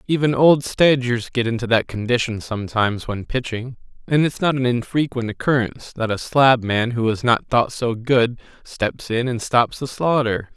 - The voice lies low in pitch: Yes, low, 120 Hz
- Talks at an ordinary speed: Yes, average, 175 wpm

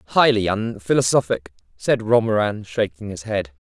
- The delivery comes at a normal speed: No, slow, 115 wpm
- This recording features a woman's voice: No, male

